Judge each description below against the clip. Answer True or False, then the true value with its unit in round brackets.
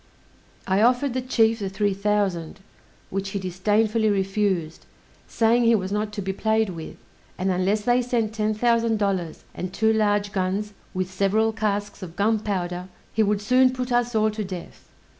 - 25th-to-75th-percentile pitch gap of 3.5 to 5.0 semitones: False (2.5 semitones)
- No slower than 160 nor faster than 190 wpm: True (170 wpm)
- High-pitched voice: True (210 Hz)